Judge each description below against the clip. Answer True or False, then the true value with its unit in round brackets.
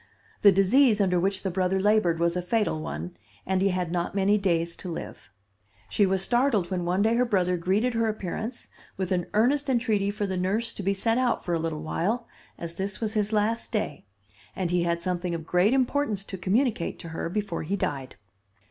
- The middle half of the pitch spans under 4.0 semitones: True (3.6 semitones)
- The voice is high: True (195 Hz)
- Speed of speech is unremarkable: False (210 wpm)